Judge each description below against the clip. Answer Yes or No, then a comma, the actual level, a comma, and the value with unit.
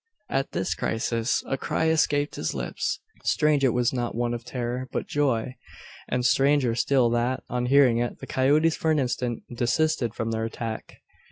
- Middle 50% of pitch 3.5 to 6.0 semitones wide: No, average, 2.9 semitones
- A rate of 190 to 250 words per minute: No, average, 175 wpm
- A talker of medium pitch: No, low, 125 Hz